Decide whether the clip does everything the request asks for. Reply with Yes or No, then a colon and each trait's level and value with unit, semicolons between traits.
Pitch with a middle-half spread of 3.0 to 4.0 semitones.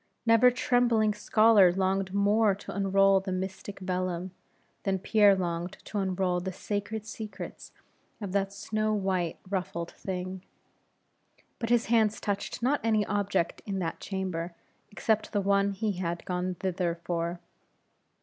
No: narrow, 2.5 semitones